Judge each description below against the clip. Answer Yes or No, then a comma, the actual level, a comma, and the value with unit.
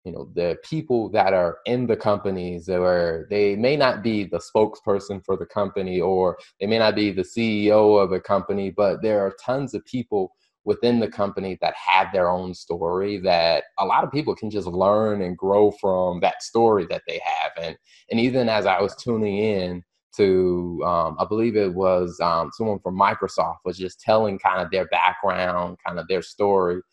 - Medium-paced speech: Yes, average, 195 wpm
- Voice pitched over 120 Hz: No, low, 100 Hz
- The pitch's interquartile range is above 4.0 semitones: No, average, 3.1 semitones